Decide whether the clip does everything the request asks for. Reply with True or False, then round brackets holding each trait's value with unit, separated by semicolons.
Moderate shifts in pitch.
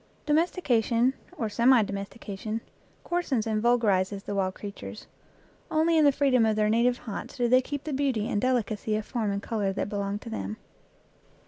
True (3.8 semitones)